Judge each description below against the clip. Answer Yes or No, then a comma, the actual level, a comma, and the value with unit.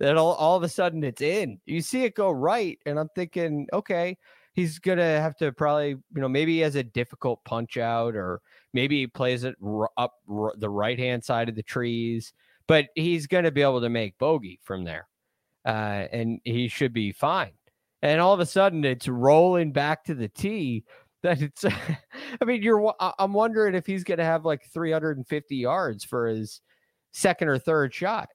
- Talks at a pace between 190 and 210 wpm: Yes, average, 195 wpm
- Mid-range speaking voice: Yes, medium, 145 Hz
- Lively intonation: Yes, wide, 6.4 semitones